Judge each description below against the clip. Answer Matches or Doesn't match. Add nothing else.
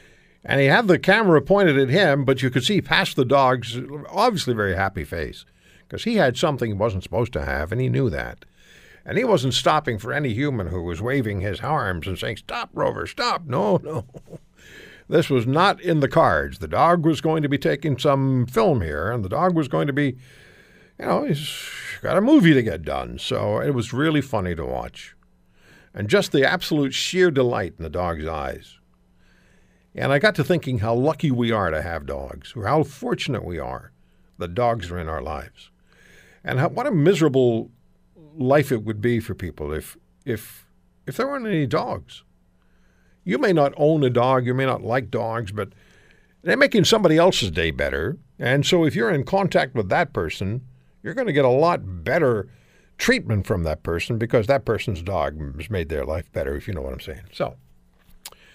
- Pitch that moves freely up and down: Matches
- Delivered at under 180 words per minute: Doesn't match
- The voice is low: Matches